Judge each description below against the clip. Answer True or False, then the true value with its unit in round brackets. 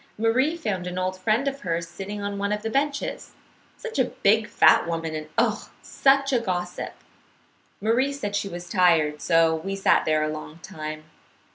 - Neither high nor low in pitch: False (195 Hz)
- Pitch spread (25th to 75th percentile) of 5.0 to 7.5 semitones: True (5.3 semitones)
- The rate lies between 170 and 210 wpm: True (180 wpm)